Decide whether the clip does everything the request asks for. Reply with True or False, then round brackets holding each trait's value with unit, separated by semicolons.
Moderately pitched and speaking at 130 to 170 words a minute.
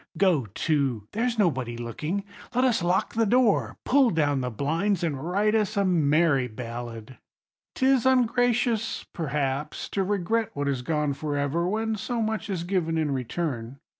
True (170 Hz; 160 wpm)